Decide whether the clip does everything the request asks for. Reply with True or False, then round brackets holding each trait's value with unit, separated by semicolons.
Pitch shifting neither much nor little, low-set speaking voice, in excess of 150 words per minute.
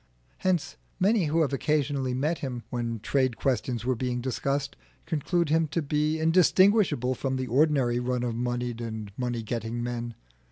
True (4.1 semitones; 130 Hz; 160 wpm)